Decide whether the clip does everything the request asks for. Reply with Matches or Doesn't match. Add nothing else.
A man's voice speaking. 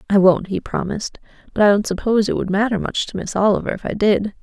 Doesn't match